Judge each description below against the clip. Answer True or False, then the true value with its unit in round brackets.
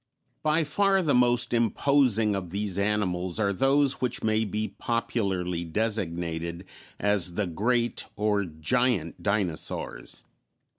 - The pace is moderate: False (120 wpm)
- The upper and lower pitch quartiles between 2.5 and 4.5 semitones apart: False (5.0 semitones)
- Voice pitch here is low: True (105 Hz)